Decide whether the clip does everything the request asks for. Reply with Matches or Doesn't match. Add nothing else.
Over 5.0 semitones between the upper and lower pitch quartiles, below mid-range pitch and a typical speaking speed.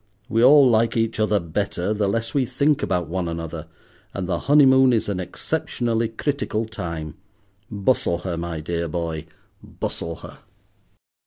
Matches